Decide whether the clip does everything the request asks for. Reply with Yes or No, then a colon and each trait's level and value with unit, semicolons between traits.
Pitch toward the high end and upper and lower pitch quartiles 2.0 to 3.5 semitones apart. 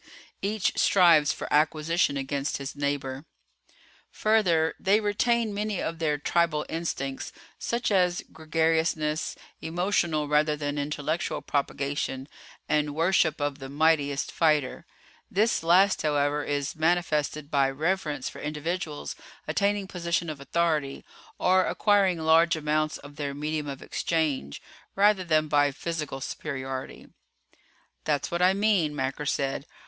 No: medium, 155 Hz; average, 3.2 semitones